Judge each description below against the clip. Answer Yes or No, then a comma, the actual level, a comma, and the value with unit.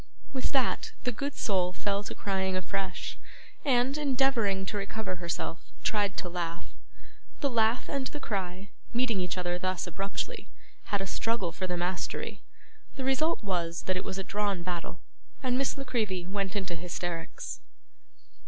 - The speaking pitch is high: Yes, high, 195 Hz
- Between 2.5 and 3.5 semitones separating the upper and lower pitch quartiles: No, average, 4.7 semitones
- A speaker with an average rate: Yes, average, 160 wpm